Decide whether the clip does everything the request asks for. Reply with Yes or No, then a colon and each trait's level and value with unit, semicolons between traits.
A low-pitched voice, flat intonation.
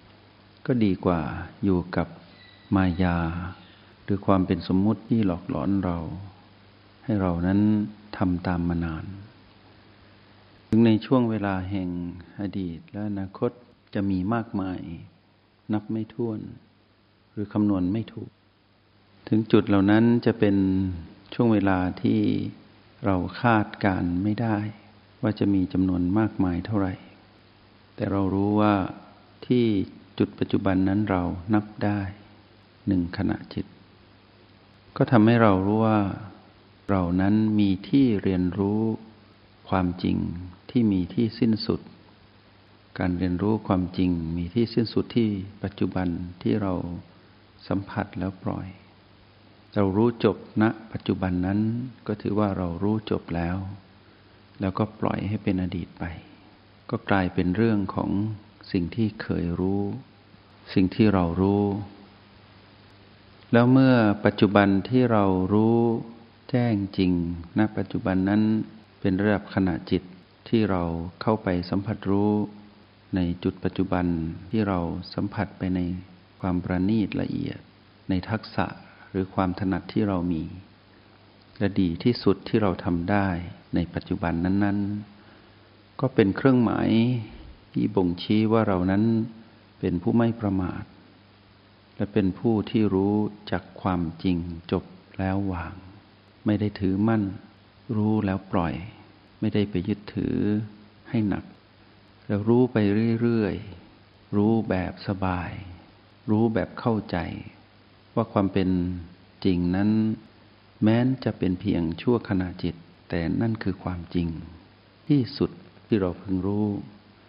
Yes: low, 100 Hz; narrow, 2.2 semitones